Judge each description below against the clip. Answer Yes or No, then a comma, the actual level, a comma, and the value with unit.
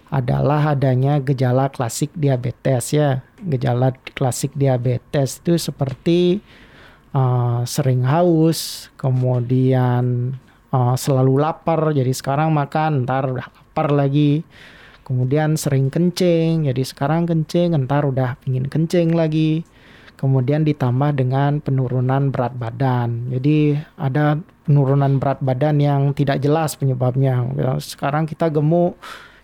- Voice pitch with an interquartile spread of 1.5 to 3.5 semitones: Yes, average, 2.8 semitones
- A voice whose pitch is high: No, medium, 140 Hz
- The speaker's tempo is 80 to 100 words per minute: No, average, 110 wpm